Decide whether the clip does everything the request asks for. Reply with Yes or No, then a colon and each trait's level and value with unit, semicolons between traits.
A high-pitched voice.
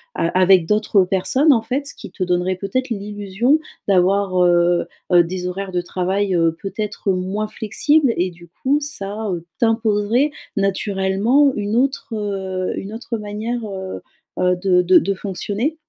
Yes: high, 200 Hz